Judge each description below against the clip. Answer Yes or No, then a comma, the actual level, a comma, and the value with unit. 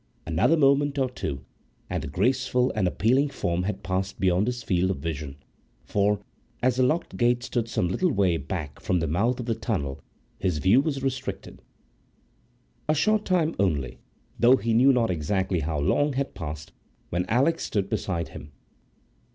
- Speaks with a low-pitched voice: Yes, low, 105 Hz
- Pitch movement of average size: No, wide, 6.9 semitones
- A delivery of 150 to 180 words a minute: Yes, average, 165 wpm